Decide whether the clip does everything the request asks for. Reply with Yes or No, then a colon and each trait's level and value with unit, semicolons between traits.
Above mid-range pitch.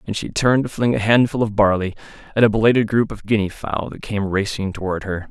No: low, 105 Hz